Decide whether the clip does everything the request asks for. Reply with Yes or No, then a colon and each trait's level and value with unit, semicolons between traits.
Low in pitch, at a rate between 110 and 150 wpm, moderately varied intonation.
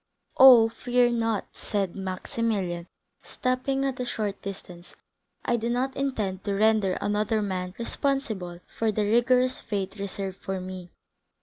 No: high, 215 Hz; slow, 135 wpm; average, 4.0 semitones